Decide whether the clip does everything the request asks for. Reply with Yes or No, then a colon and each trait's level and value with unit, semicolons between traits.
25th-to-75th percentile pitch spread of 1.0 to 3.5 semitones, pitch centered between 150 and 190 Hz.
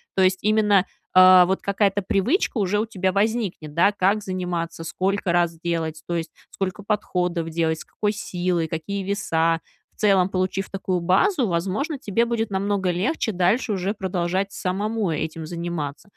Yes: average, 3.0 semitones; medium, 185 Hz